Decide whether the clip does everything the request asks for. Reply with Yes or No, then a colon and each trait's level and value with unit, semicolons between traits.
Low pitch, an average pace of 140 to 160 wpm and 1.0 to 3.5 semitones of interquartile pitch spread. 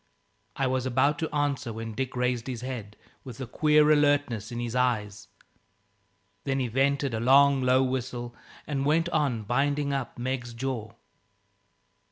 Yes: low, 130 Hz; average, 155 wpm; average, 2.8 semitones